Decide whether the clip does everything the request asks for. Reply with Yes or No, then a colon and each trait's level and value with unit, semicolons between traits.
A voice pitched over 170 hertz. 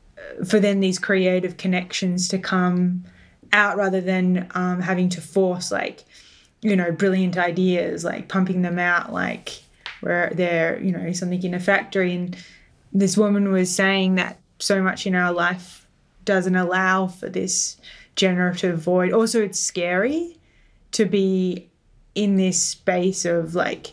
Yes: medium, 185 Hz